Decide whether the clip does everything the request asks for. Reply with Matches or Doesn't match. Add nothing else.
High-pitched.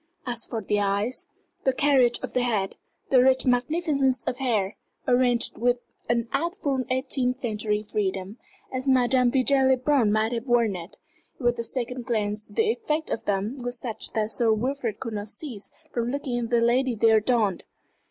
Matches